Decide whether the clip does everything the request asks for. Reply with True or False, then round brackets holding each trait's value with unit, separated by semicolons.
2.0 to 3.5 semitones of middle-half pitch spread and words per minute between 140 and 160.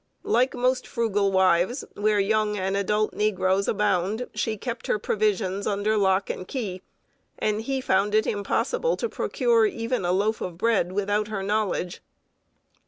True (2.5 semitones; 155 wpm)